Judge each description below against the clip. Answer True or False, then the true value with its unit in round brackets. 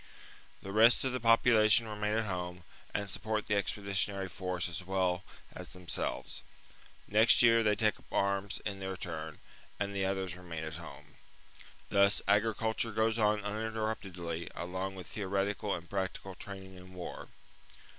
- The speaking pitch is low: True (100 Hz)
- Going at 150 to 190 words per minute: True (155 wpm)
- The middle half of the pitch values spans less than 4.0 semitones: True (2.6 semitones)